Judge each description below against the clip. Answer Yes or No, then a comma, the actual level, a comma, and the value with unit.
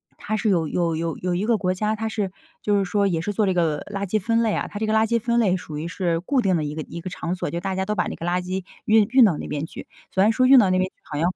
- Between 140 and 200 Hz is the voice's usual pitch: Yes, high, 190 Hz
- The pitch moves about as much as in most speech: Yes, average, 3.9 semitones